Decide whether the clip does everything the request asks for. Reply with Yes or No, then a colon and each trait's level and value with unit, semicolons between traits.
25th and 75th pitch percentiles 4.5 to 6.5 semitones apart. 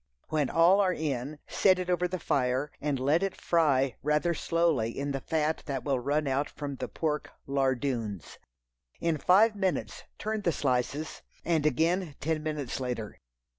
No: average, 4.0 semitones